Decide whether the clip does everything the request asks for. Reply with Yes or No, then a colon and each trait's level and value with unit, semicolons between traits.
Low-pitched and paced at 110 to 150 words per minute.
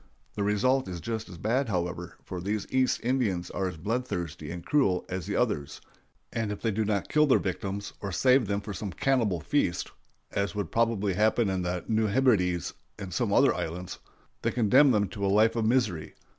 No: low, 100 Hz; average, 200 wpm